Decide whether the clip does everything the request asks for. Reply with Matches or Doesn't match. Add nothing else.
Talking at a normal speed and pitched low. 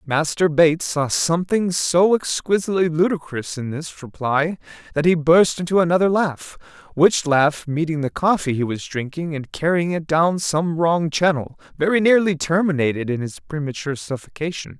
Doesn't match